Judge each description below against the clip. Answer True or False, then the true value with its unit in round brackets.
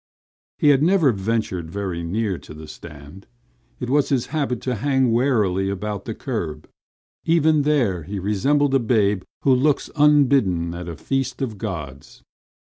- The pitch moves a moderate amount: False (6.9 semitones)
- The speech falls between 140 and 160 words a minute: True (155 wpm)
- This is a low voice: True (110 Hz)